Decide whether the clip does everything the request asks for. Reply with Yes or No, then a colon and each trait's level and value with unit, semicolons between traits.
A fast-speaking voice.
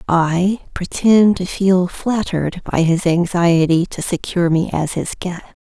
No: average, 150 wpm